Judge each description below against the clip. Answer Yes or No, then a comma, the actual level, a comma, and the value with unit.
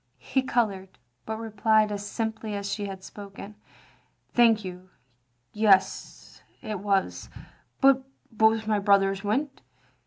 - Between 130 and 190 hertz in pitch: No, high, 210 Hz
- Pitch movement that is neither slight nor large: No, narrow, 1.9 semitones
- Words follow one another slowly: Yes, slow, 125 wpm